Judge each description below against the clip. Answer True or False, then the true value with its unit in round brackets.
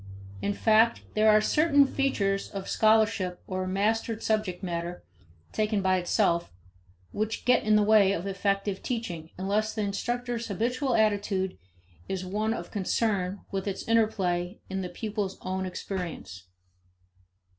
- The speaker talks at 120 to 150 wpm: True (135 wpm)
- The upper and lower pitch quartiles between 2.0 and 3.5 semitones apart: True (2.8 semitones)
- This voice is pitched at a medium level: False (205 Hz)